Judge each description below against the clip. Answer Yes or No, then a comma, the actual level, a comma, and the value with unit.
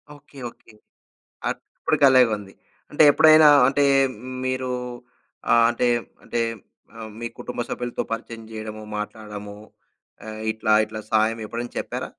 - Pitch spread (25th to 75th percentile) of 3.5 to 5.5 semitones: No, average, 2.9 semitones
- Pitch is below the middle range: Yes, low, 115 Hz